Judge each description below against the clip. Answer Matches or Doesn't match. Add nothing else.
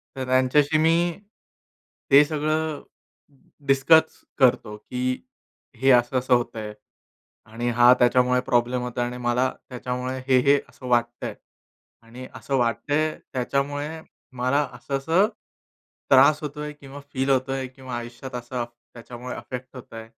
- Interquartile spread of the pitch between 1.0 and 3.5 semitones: Matches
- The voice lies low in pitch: Matches